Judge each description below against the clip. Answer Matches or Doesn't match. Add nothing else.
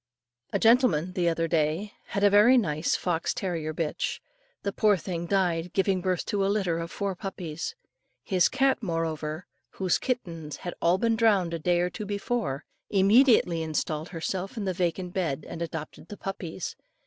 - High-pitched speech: Doesn't match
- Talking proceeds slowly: Doesn't match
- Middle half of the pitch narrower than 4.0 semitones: Matches